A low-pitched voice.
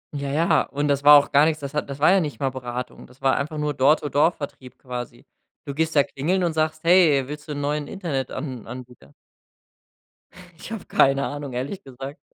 No: medium, 145 Hz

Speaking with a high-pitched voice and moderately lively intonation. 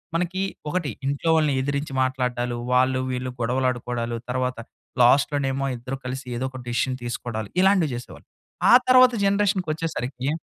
No: low, 130 Hz; average, 3.7 semitones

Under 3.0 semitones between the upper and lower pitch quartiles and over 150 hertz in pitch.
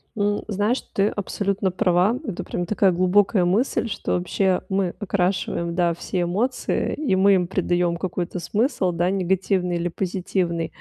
Yes: narrow, 2.4 semitones; medium, 185 Hz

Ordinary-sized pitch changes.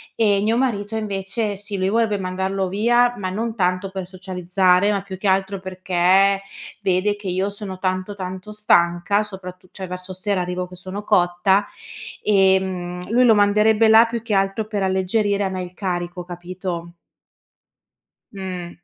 No: narrow, 2.0 semitones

